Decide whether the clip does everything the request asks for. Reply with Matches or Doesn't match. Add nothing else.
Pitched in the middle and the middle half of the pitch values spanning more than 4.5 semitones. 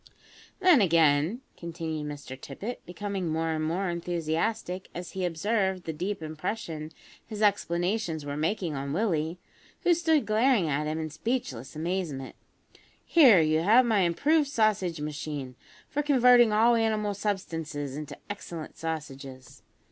Matches